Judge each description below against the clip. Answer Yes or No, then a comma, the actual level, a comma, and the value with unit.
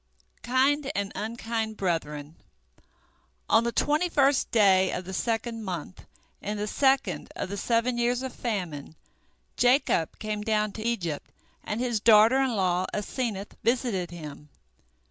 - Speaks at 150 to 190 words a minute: No, average, 140 wpm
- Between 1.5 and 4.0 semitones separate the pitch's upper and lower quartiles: No, average, 4.5 semitones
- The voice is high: Yes, high, 220 Hz